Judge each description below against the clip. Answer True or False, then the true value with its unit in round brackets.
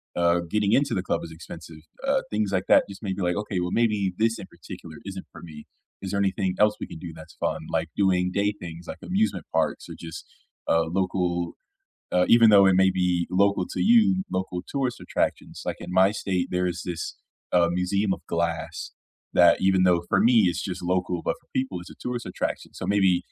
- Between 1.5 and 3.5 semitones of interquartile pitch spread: True (2.7 semitones)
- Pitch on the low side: True (95 Hz)